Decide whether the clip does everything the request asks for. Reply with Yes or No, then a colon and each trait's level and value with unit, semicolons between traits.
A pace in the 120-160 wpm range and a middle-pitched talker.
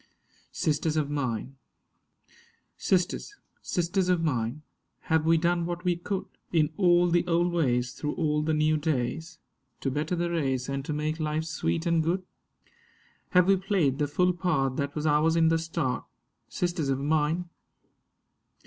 Yes: average, 155 wpm; medium, 160 Hz